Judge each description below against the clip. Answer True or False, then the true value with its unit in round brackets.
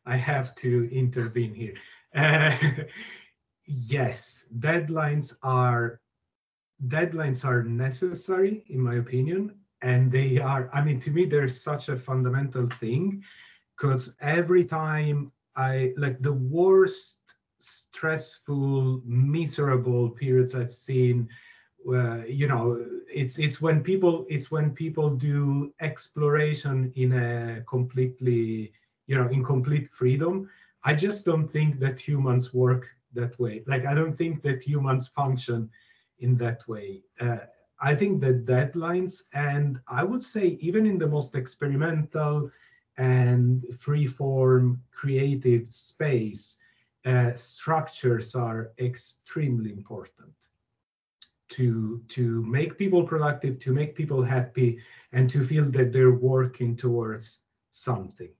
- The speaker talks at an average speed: False (120 wpm)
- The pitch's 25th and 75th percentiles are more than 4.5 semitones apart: False (3.4 semitones)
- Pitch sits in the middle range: False (130 Hz)